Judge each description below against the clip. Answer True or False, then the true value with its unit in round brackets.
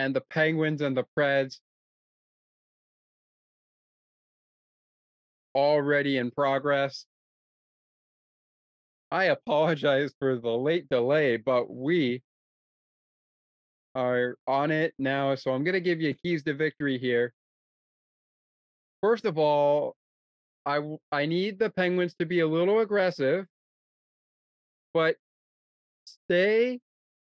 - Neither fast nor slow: False (100 wpm)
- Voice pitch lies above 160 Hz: False (145 Hz)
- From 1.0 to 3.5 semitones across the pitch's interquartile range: False (4.0 semitones)